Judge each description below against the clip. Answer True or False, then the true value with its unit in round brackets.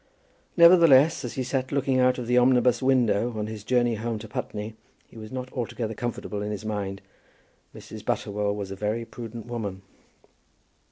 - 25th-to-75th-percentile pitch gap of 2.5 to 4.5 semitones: True (3.2 semitones)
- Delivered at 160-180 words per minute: True (170 wpm)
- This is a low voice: True (115 Hz)